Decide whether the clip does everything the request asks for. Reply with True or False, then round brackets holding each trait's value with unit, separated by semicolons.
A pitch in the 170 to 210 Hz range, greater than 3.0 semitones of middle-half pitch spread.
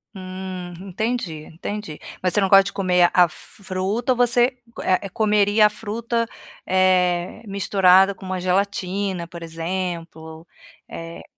False (185 Hz; 2.5 semitones)